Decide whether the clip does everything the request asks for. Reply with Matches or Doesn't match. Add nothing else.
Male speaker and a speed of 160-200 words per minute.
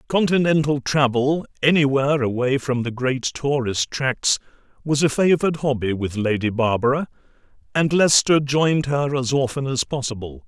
Doesn't match